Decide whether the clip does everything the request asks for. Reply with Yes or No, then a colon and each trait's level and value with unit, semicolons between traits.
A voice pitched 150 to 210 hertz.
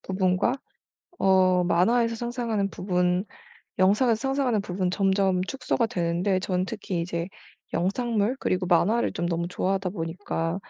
Yes: high, 190 Hz